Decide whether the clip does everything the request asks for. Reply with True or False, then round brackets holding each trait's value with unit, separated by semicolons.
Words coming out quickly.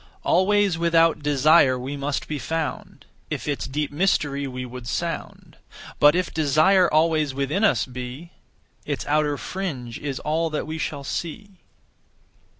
False (145 wpm)